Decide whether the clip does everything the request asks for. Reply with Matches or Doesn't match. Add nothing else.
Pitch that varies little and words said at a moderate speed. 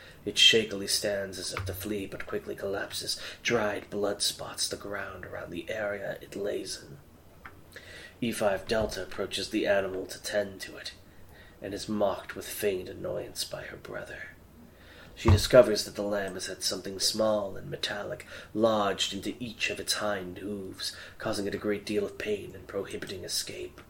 Matches